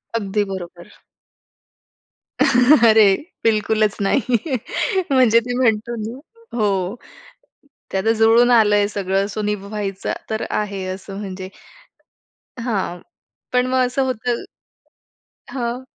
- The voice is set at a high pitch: Yes, high, 215 Hz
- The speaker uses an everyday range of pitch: Yes, average, 3.4 semitones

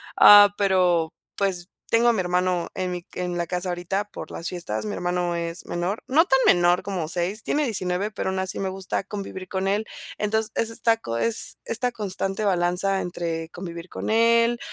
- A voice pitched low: No, high, 190 Hz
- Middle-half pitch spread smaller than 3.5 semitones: Yes, average, 3.1 semitones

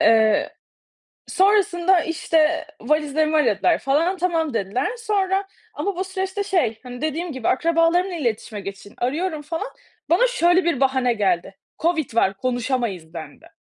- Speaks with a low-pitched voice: No, very high, 310 Hz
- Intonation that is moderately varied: No, wide, 6.8 semitones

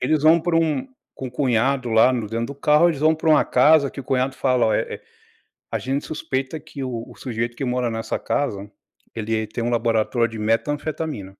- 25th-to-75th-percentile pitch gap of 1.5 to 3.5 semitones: No, average, 4.2 semitones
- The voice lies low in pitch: Yes, low, 130 Hz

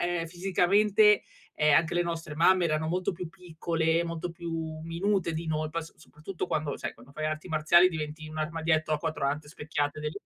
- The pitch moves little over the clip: Yes, narrow, 2.2 semitones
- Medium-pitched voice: Yes, medium, 165 Hz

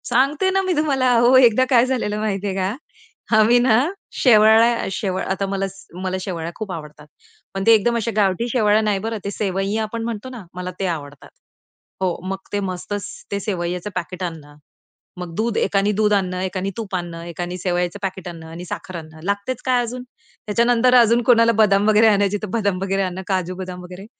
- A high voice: Yes, high, 200 Hz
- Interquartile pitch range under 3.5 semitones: No, average, 3.8 semitones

